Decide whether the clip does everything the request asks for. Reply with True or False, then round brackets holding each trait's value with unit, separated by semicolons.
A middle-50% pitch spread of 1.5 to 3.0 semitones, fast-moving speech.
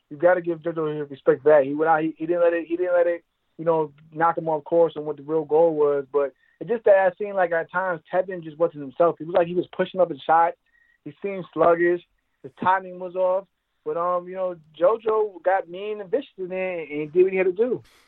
True (2.7 semitones; 255 wpm)